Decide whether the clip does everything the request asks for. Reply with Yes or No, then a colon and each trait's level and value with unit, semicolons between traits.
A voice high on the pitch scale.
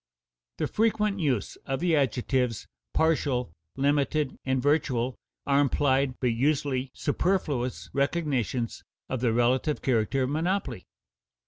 No: low, 135 Hz